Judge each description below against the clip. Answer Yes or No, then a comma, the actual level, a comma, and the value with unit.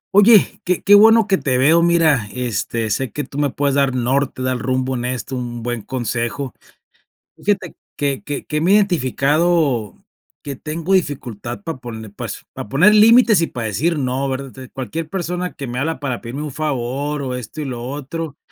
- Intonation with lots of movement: No, average, 4.7 semitones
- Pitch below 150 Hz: Yes, medium, 140 Hz